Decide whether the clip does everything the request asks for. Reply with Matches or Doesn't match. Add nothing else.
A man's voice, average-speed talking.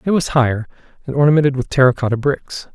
Matches